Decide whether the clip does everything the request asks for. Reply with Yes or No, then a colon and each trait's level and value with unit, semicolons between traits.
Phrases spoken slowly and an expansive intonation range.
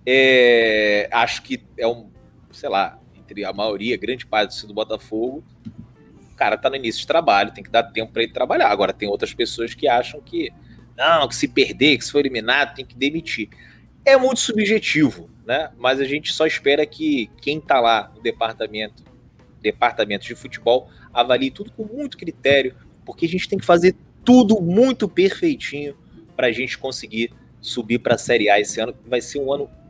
No: fast, 185 wpm; wide, 9.0 semitones